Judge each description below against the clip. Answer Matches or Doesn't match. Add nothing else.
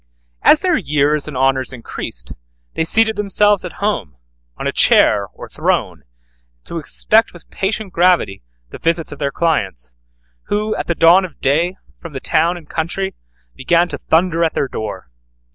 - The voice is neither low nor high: Matches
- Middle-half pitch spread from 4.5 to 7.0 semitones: Matches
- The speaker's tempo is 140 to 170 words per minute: Matches